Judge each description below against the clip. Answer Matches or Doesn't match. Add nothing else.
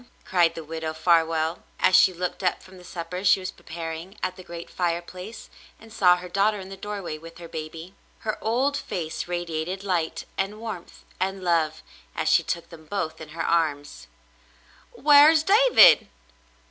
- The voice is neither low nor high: Matches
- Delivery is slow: Doesn't match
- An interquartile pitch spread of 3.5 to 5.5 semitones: Doesn't match